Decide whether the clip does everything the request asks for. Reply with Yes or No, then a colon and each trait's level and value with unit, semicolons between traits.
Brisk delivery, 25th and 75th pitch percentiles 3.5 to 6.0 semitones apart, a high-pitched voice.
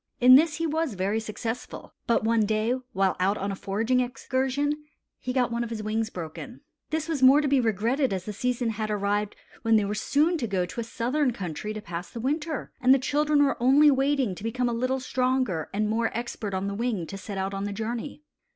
Yes: fast, 225 wpm; average, 4.3 semitones; high, 235 Hz